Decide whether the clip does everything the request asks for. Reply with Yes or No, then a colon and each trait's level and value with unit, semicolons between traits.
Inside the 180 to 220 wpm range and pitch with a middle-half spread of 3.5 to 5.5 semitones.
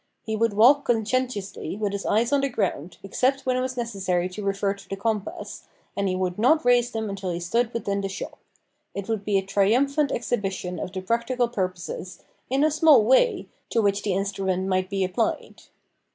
Yes: average, 195 wpm; average, 4.0 semitones